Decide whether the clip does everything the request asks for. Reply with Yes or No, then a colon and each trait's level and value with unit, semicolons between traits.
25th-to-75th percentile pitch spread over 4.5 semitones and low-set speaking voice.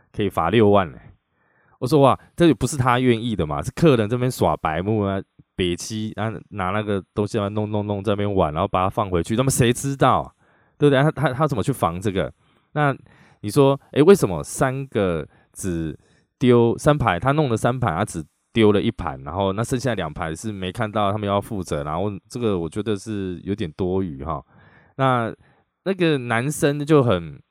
Yes: wide, 5.5 semitones; low, 110 Hz